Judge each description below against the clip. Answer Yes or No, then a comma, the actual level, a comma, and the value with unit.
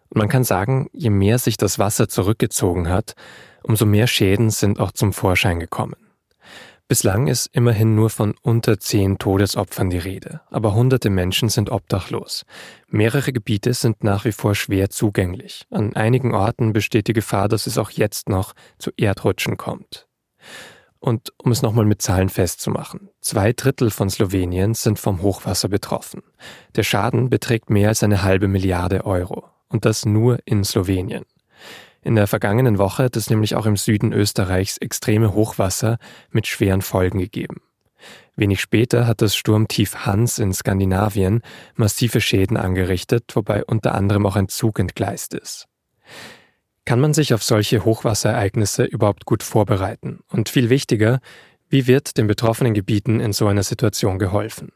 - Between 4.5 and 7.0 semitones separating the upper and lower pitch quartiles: No, average, 3.0 semitones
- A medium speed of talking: Yes, average, 155 wpm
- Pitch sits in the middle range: No, low, 110 Hz